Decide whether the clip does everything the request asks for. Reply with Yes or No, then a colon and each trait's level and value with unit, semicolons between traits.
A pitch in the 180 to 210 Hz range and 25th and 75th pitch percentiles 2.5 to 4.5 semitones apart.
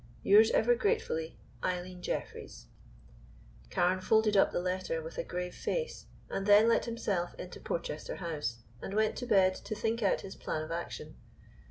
Yes: medium, 185 Hz; average, 3.9 semitones